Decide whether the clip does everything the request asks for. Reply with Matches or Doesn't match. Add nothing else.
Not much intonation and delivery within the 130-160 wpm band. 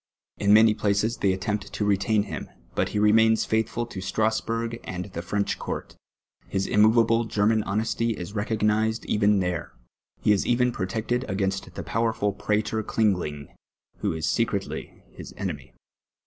Matches